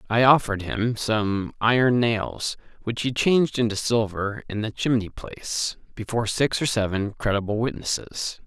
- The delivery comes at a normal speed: Yes, average, 150 wpm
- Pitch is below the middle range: Yes, low, 110 Hz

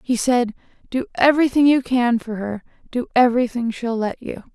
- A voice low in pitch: No, high, 240 Hz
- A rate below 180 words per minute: Yes, average, 170 wpm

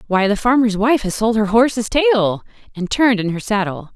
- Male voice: No, female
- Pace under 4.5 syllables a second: No, 5.9 syllables/s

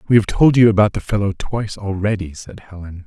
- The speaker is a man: Yes, male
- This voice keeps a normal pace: No, fast, 215 wpm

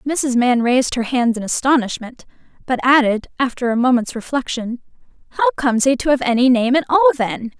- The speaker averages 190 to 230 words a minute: No, average, 180 wpm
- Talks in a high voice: Yes, high, 245 Hz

